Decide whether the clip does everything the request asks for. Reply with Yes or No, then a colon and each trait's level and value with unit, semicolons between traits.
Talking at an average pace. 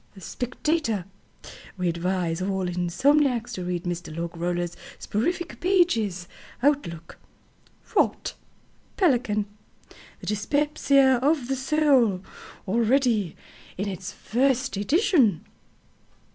No: slow, 90 wpm